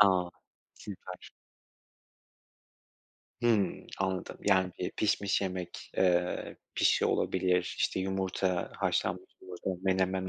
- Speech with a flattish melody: Yes, narrow, 1.0 semitones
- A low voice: Yes, very low, 95 Hz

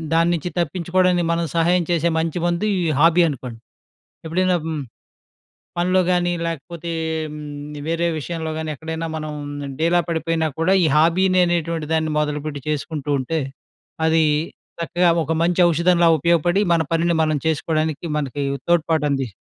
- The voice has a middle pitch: Yes, medium, 165 Hz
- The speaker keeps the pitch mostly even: Yes, narrow, 1.8 semitones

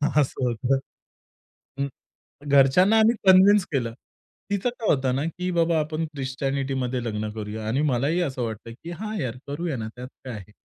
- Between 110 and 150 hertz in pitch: Yes, low, 135 Hz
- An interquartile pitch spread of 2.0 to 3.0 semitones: No, wide, 5.6 semitones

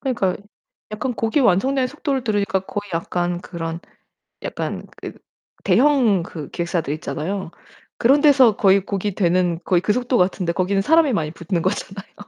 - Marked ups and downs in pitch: Yes, wide, 5.8 semitones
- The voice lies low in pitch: No, high, 195 Hz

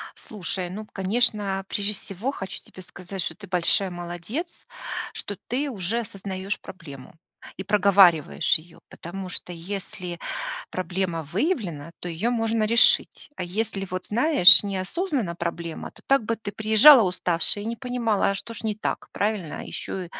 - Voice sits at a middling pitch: No, high, 195 Hz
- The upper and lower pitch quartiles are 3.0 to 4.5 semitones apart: Yes, average, 3.6 semitones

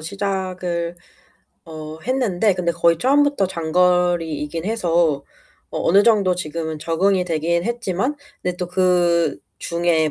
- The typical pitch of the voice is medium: Yes, medium, 175 Hz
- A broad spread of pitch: No, narrow, 2.6 semitones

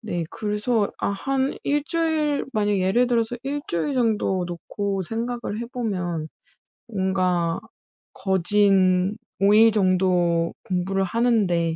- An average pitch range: Yes, average, 4.4 semitones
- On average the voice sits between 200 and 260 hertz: Yes, high, 205 Hz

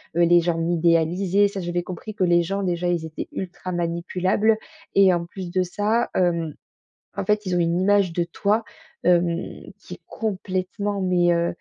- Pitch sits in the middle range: Yes, medium, 180 Hz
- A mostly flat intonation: Yes, narrow, 2.3 semitones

